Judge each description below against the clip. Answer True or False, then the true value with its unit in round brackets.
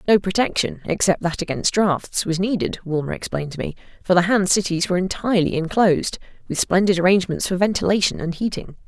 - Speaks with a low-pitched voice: False (185 Hz)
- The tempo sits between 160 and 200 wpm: True (175 wpm)